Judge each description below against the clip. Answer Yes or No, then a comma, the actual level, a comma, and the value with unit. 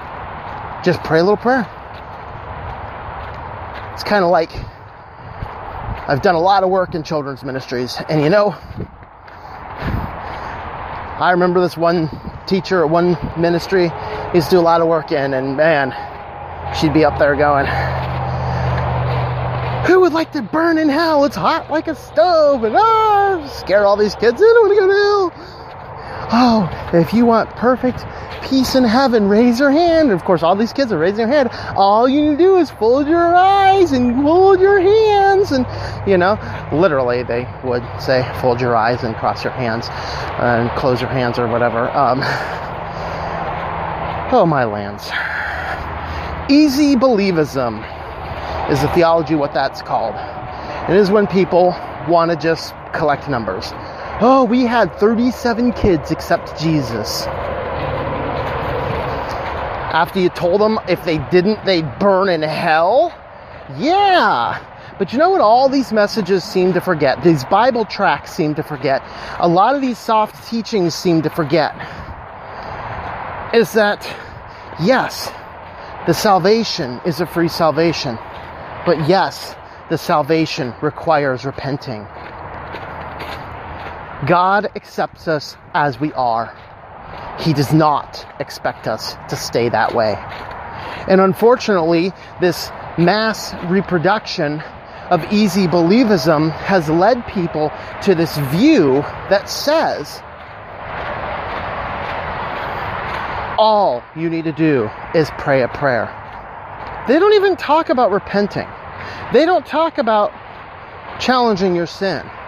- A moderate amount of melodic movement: No, wide, 8.6 semitones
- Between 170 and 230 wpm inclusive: No, average, 140 wpm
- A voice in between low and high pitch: Yes, medium, 180 Hz